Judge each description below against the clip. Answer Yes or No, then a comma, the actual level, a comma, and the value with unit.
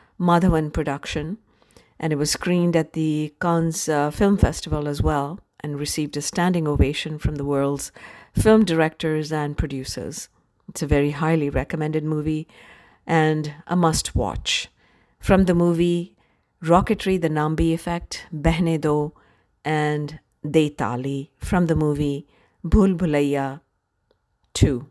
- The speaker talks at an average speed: No, slow, 130 wpm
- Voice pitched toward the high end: No, medium, 155 Hz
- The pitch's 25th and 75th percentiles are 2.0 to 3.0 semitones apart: Yes, narrow, 2.6 semitones